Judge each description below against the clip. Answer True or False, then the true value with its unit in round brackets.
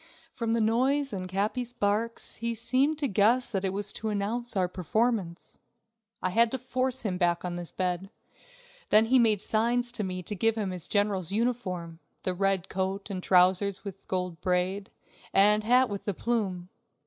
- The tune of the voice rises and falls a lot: False (4.0 semitones)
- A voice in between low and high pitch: False (205 Hz)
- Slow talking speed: False (180 wpm)